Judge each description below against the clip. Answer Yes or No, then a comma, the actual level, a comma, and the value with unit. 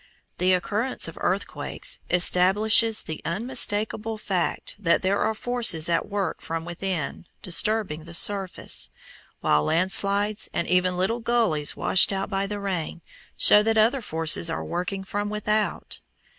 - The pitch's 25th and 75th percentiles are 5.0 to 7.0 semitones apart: No, average, 3.7 semitones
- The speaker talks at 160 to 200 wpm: No, average, 145 wpm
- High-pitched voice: Yes, high, 195 Hz